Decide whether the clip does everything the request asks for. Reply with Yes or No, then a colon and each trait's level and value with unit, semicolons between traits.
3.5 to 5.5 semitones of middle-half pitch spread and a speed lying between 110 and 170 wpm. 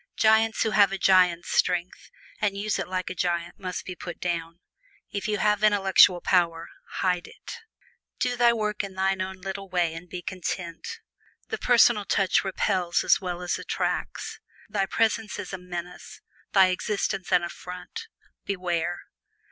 No: narrow, 2.6 semitones; average, 165 wpm